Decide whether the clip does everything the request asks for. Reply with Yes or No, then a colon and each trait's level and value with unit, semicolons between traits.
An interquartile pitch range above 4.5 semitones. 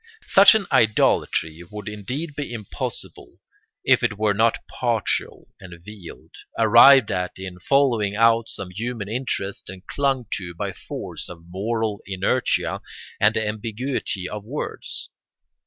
No: average, 3.9 semitones